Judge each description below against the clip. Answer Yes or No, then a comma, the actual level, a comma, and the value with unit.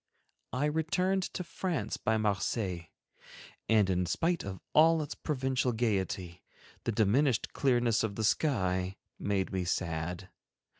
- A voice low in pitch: Yes, low, 110 Hz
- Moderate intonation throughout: No, wide, 7.4 semitones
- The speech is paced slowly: Yes, slow, 130 wpm